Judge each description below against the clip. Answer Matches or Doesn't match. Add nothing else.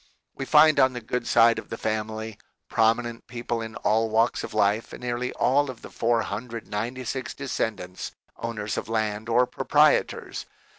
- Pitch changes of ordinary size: Doesn't match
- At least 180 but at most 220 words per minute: Doesn't match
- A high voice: Doesn't match